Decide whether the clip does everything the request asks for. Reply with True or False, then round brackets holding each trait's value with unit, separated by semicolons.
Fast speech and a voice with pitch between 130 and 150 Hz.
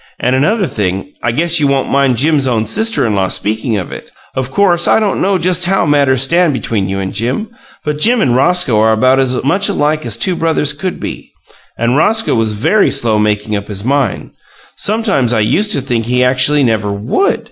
True (210 wpm; 135 Hz)